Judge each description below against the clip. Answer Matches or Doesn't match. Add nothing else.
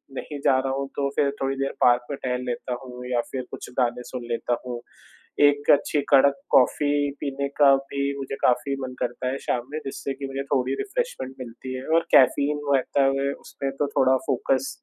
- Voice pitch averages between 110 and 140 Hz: Matches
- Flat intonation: Matches